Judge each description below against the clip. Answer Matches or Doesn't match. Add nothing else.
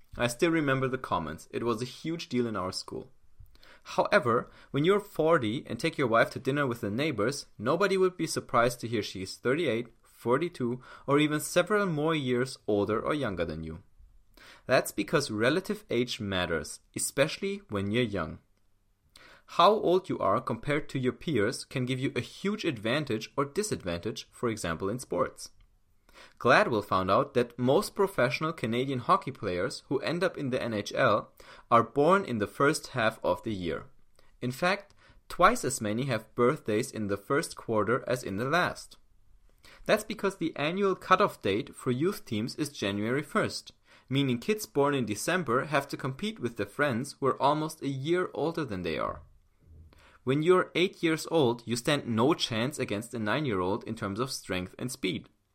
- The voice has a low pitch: Matches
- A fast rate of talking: Doesn't match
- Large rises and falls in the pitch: Matches